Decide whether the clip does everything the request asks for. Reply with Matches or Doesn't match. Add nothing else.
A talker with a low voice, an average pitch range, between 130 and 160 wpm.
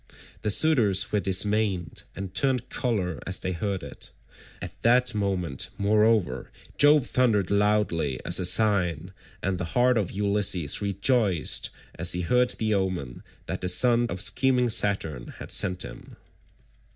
Matches